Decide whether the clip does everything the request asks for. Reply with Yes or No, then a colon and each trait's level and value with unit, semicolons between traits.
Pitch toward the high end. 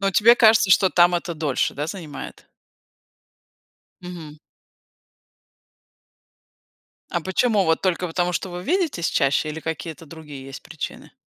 No: medium, 175 Hz